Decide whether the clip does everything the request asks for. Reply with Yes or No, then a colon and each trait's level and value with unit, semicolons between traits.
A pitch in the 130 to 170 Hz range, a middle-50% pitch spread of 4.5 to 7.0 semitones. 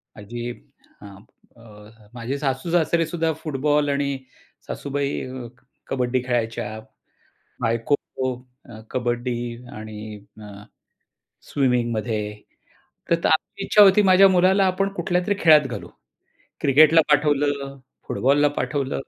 Yes: medium, 140 Hz; average, 5.1 semitones